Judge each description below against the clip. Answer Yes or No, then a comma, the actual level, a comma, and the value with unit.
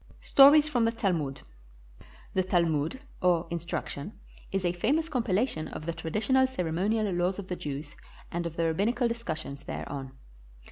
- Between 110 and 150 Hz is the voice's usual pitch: No, medium, 180 Hz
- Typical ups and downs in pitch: No, wide, 6.1 semitones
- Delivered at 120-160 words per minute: Yes, average, 150 wpm